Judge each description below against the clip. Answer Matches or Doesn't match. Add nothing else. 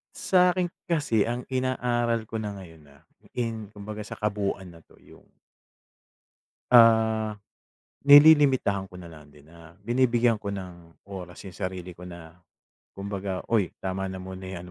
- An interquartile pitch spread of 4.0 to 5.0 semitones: Matches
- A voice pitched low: Matches